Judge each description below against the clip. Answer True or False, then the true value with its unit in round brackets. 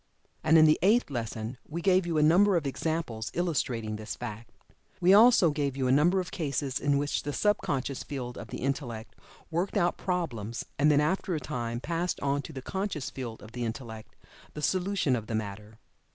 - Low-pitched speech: False (145 Hz)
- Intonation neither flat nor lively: False (6.2 semitones)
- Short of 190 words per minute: False (200 wpm)